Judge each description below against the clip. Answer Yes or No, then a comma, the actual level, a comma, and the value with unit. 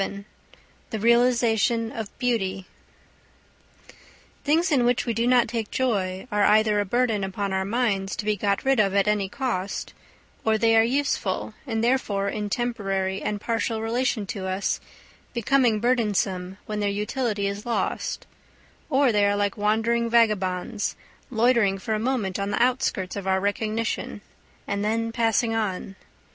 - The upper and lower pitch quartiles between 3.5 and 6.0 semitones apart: No, average, 2.9 semitones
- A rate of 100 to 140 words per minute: No, average, 155 wpm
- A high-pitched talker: Yes, high, 215 Hz